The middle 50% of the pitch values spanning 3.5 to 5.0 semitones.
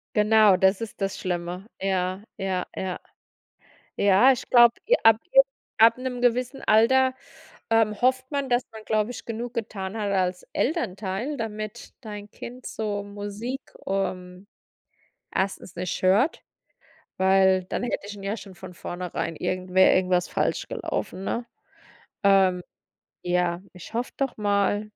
Yes: average, 4.0 semitones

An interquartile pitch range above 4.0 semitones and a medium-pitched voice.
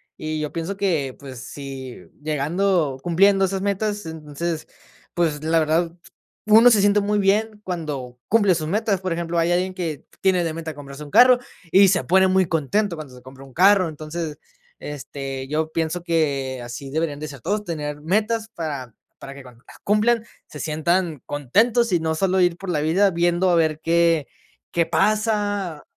Yes: average, 4.6 semitones; medium, 165 Hz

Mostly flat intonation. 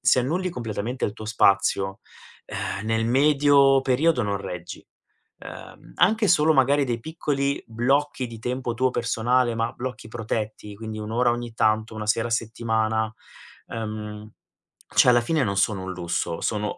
No: average, 3.4 semitones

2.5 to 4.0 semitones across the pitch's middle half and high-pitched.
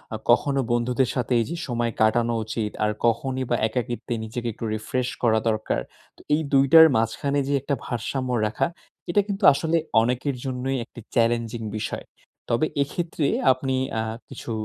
No: average, 3.0 semitones; low, 125 Hz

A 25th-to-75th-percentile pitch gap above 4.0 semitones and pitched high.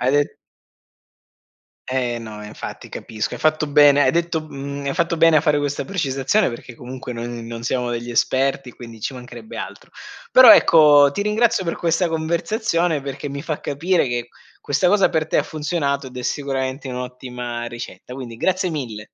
No: average, 4.6 semitones; medium, 140 Hz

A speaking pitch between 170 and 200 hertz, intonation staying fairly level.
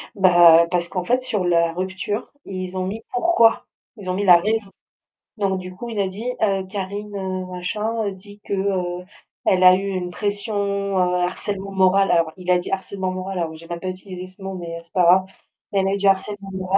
Yes: high, 190 Hz; narrow, 1.7 semitones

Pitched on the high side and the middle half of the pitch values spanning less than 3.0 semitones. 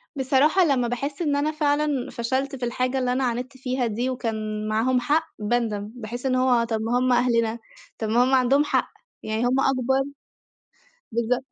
Yes: very high, 250 Hz; narrow, 2.5 semitones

